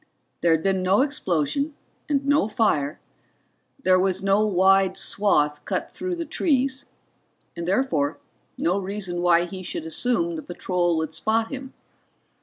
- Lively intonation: Yes, wide, 6.3 semitones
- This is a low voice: No, high, 190 Hz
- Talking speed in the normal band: Yes, average, 145 wpm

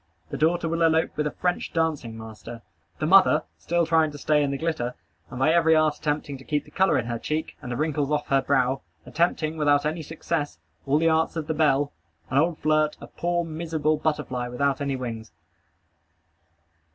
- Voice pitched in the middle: Yes, medium, 150 Hz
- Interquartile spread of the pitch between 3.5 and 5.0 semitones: No, average, 2.9 semitones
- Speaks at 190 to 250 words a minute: Yes, average, 200 wpm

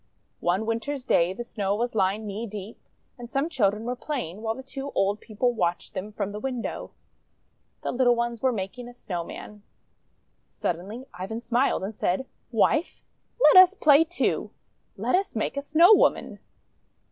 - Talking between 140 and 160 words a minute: No, average, 170 wpm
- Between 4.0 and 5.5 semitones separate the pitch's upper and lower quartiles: Yes, average, 4.6 semitones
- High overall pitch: Yes, high, 230 Hz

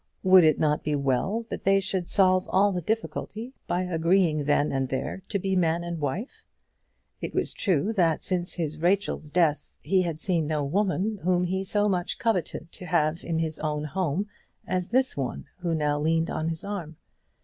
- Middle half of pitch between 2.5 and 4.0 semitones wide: Yes, average, 3.6 semitones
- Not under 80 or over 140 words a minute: No, average, 185 wpm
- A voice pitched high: No, medium, 175 Hz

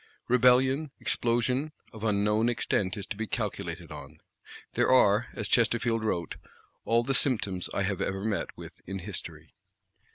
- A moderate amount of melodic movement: Yes, average, 3.6 semitones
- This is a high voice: No, low, 110 Hz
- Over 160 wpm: No, average, 150 wpm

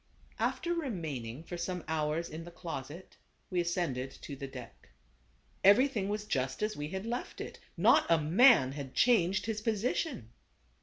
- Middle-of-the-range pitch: Yes, medium, 175 Hz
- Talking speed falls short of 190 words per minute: Yes, average, 155 wpm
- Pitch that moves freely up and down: Yes, wide, 6.3 semitones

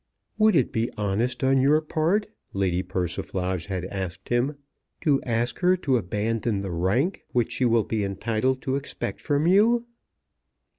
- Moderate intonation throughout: No, wide, 6.7 semitones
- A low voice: Yes, low, 120 Hz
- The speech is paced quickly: No, average, 155 wpm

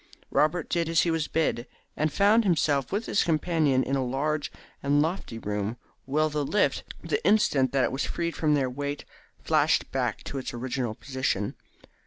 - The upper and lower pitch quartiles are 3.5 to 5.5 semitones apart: Yes, average, 3.9 semitones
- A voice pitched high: No, medium, 145 Hz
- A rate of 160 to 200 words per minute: Yes, average, 180 wpm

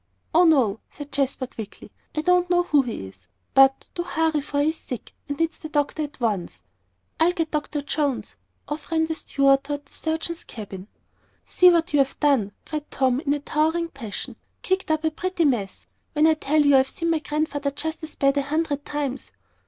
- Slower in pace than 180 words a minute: No, average, 195 wpm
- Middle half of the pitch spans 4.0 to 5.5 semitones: No, average, 2.8 semitones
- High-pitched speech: Yes, very high, 295 Hz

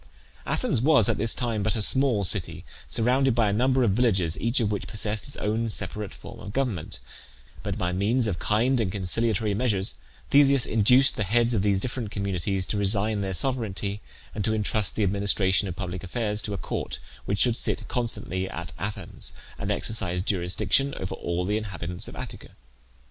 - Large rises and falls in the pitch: No, average, 3.5 semitones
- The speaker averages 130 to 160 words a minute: No, average, 185 wpm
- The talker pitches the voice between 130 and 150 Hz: No, low, 105 Hz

